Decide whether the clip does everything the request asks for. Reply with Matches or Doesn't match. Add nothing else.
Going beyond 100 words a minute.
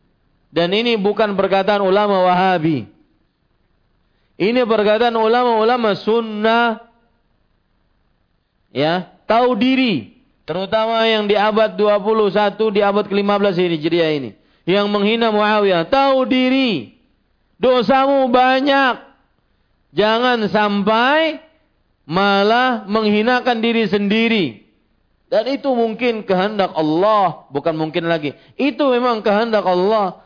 Doesn't match